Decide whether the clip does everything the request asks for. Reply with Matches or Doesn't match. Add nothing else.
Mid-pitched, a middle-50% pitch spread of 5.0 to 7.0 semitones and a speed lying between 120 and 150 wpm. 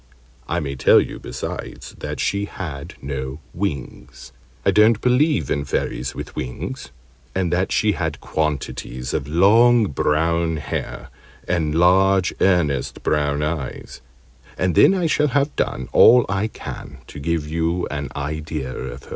Doesn't match